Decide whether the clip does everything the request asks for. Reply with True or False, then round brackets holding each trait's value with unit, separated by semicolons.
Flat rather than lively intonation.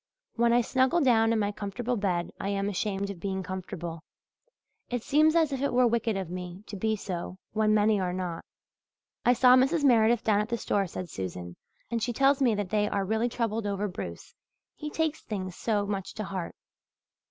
False (3.9 semitones)